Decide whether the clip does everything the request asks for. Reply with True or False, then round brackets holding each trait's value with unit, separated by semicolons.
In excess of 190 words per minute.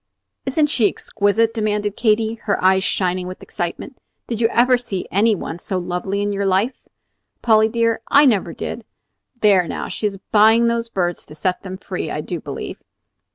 False (180 wpm)